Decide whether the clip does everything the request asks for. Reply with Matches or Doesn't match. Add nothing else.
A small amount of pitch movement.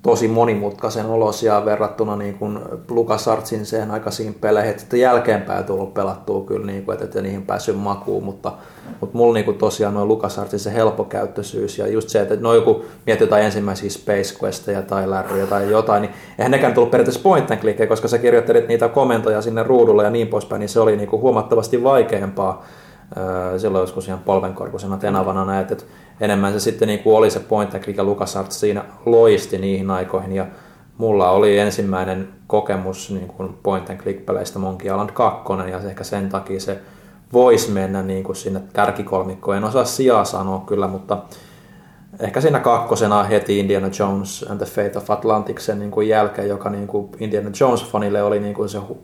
Matches